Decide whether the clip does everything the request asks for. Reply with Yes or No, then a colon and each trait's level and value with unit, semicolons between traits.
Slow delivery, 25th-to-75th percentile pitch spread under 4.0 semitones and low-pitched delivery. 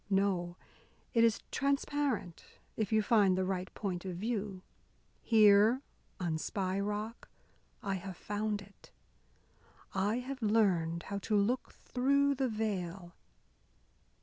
No: slow, 120 wpm; average, 3.3 semitones; high, 205 Hz